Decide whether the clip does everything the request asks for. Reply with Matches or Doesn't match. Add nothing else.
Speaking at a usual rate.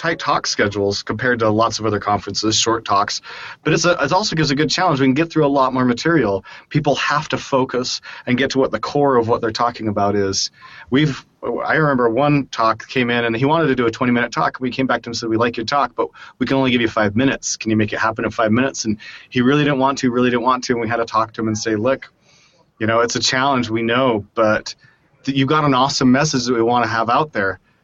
Doesn't match